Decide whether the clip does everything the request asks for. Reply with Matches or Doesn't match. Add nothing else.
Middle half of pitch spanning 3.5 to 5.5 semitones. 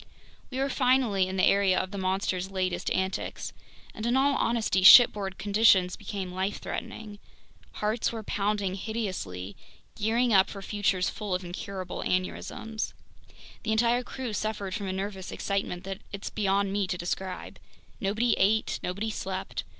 Doesn't match